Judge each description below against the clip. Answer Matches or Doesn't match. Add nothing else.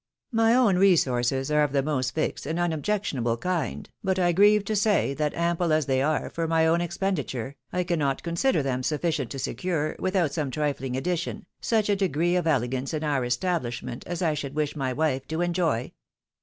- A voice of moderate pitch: Matches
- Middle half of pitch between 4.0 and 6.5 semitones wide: Matches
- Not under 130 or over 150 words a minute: Doesn't match